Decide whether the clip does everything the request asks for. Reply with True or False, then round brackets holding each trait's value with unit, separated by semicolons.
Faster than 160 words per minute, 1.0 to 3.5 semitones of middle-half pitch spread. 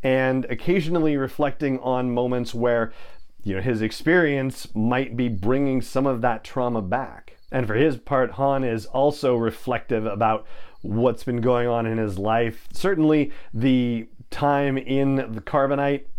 False (150 wpm; 3.0 semitones)